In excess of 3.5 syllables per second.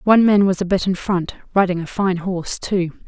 Yes: 5.5 syllables/s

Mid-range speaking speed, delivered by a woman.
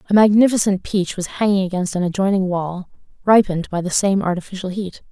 Yes: average, 175 wpm; female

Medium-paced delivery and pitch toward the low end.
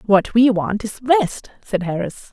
No: average, 180 wpm; high, 215 Hz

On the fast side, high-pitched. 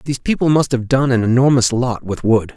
No: fast, 235 wpm; low, 125 Hz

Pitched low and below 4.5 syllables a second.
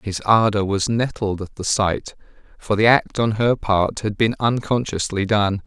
Yes: low, 105 Hz; 4.3 syllables/s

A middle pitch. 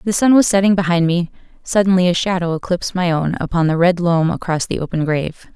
Yes: medium, 175 Hz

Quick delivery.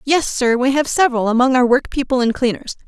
Yes: fast, 210 wpm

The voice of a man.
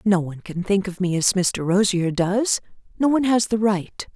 No: female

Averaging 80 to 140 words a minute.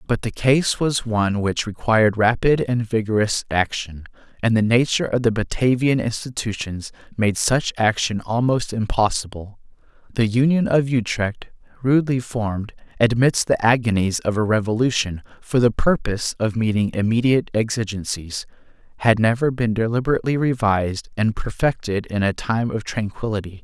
Yes: slow, 135 wpm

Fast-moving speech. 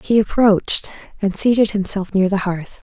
No: average, 165 wpm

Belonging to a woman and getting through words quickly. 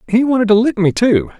No: male; fast, 260 wpm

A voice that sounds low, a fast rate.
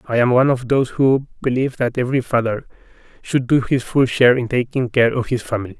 Yes: low, 125 Hz; fast, 240 wpm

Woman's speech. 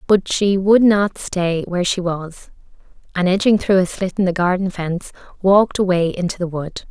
Yes: female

